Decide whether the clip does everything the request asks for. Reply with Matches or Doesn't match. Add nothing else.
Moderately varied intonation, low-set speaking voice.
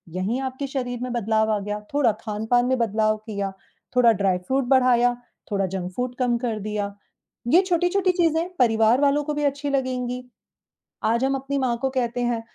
Doesn't match